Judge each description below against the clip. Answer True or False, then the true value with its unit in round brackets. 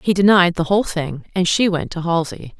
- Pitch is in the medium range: True (175 Hz)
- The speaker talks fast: True (230 wpm)